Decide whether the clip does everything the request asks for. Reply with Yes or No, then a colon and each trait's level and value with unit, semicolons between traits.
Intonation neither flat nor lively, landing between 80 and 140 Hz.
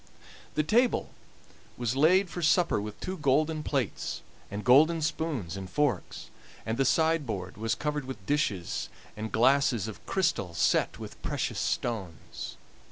No: wide, 6.6 semitones; low, 135 Hz